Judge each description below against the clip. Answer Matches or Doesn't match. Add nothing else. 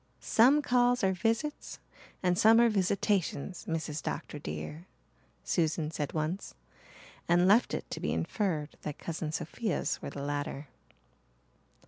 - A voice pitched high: Doesn't match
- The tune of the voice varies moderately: Doesn't match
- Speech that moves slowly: Matches